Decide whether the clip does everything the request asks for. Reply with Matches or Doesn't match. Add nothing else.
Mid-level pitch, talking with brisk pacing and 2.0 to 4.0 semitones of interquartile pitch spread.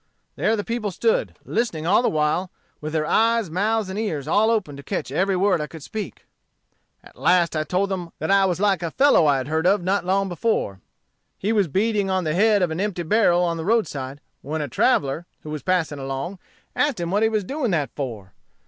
Doesn't match